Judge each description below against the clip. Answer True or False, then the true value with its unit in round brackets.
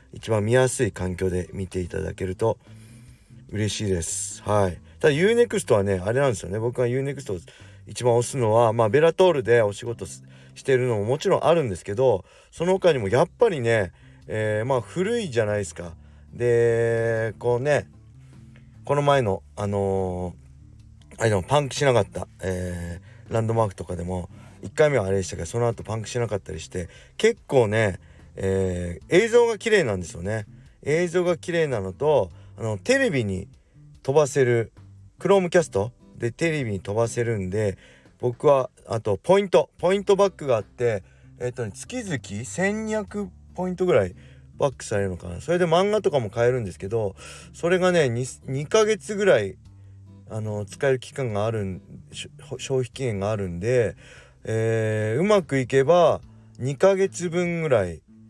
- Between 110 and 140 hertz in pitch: True (115 Hz)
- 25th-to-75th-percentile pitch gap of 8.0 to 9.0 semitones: False (6.3 semitones)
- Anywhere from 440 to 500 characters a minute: False (335 characters per minute)